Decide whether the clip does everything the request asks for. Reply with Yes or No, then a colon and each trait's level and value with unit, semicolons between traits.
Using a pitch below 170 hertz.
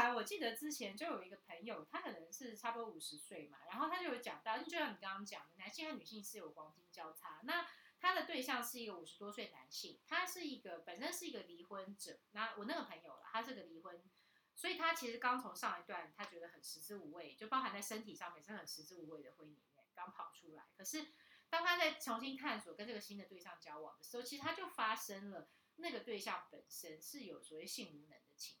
No: high, 220 Hz